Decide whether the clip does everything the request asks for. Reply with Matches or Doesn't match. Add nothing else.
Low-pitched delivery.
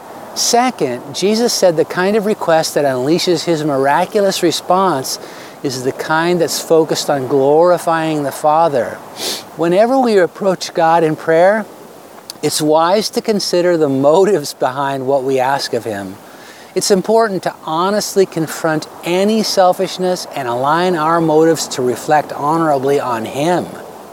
Doesn't match